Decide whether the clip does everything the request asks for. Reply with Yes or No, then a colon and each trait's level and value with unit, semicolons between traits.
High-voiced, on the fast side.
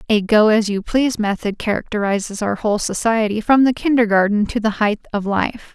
No: high, 215 Hz; average, 190 wpm